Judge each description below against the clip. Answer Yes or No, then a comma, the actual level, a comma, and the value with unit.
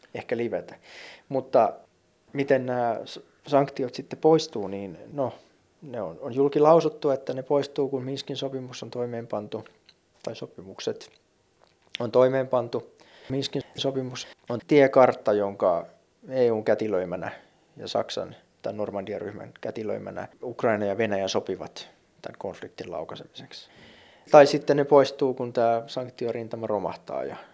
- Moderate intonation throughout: Yes, average, 3.1 semitones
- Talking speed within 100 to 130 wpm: Yes, average, 120 wpm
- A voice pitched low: Yes, low, 130 Hz